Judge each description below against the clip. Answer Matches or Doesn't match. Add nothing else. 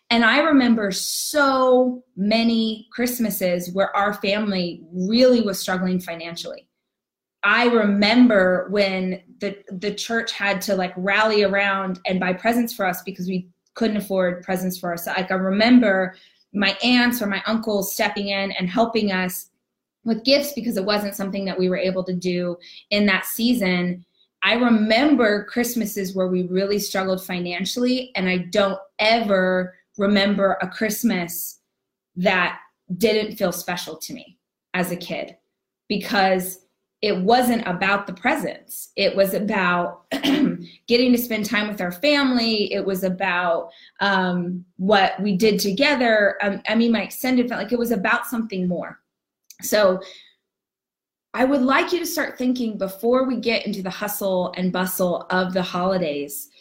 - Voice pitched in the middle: Doesn't match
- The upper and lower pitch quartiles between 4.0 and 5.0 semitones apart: Doesn't match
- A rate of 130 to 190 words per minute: Matches